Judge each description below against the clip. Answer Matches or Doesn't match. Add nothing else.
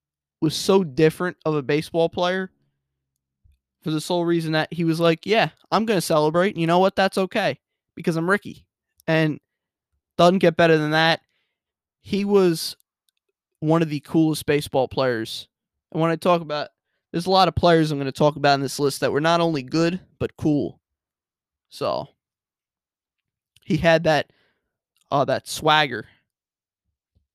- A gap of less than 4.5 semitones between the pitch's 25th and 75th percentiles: Doesn't match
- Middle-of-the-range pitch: Matches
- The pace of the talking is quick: Doesn't match